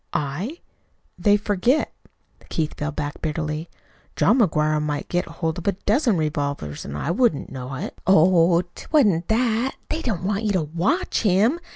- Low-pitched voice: No, medium, 175 Hz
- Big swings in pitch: Yes, wide, 5.9 semitones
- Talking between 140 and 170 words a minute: Yes, average, 160 wpm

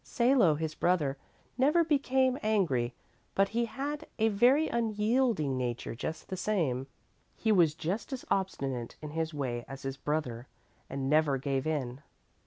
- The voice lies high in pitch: No, medium, 160 Hz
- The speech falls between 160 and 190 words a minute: No, average, 150 wpm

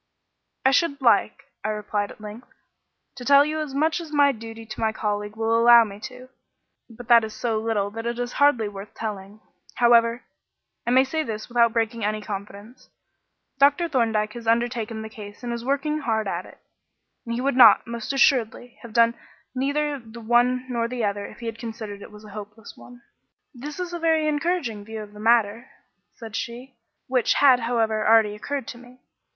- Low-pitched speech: No, high, 235 Hz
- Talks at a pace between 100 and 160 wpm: No, average, 190 wpm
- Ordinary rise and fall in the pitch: Yes, average, 3.0 semitones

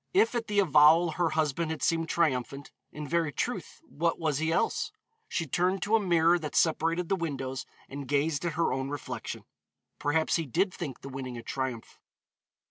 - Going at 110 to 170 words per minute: No, average, 185 wpm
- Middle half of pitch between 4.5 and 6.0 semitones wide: No, average, 3.4 semitones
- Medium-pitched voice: Yes, medium, 160 Hz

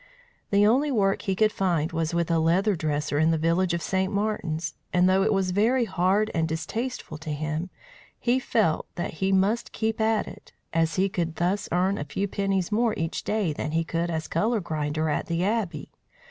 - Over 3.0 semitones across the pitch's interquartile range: Yes, average, 4.2 semitones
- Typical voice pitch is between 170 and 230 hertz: Yes, medium, 185 Hz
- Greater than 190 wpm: Yes, average, 200 wpm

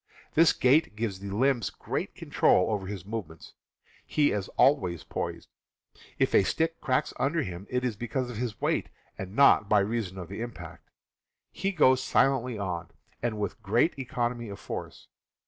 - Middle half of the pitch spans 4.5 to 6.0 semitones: Yes, average, 4.9 semitones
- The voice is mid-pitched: No, low, 115 Hz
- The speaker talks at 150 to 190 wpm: Yes, average, 165 wpm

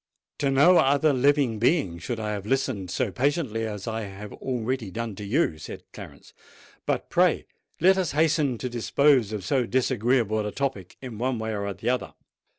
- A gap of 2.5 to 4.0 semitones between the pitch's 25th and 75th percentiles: No, average, 4.5 semitones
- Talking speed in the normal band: Yes, average, 180 wpm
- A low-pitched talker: Yes, low, 120 Hz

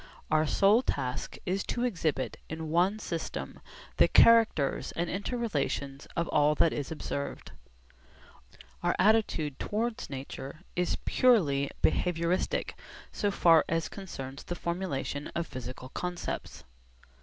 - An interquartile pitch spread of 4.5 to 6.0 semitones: Yes, wide, 5.5 semitones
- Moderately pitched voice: Yes, medium, 165 Hz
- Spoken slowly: Yes, slow, 120 wpm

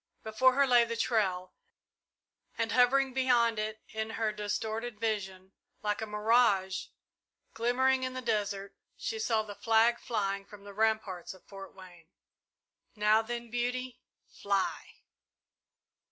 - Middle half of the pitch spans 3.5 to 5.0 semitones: No, average, 2.9 semitones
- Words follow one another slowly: Yes, slow, 130 wpm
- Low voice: No, high, 220 Hz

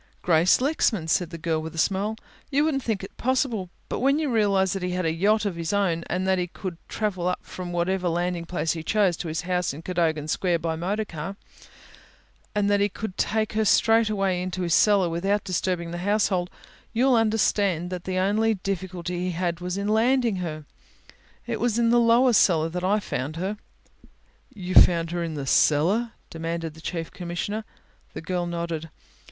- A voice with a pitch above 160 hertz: Yes, medium, 185 Hz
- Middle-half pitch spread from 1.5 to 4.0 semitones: Yes, average, 3.7 semitones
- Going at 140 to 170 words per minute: No, average, 195 wpm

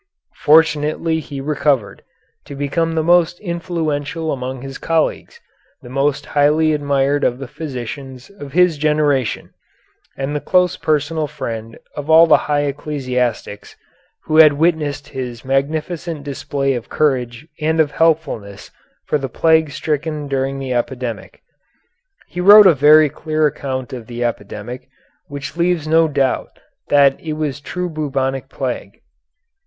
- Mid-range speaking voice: Yes, medium, 145 Hz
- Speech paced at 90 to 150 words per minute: Yes, average, 140 wpm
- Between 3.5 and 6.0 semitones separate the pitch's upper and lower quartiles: No, average, 3.0 semitones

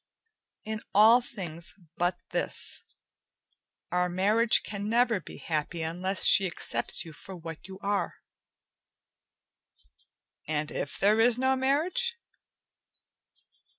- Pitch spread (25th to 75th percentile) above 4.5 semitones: Yes, average, 5.1 semitones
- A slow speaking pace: Yes, slow, 110 wpm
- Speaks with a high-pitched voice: Yes, high, 195 Hz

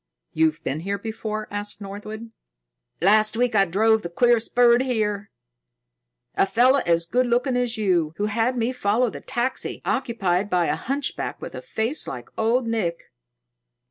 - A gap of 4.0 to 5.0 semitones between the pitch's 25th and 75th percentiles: No, average, 3.6 semitones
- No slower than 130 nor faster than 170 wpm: Yes, average, 160 wpm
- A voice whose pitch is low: No, high, 220 Hz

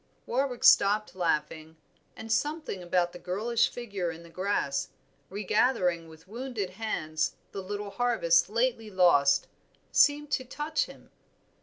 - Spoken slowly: Yes, slow, 130 wpm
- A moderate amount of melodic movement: No, wide, 5.8 semitones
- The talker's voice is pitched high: Yes, high, 200 Hz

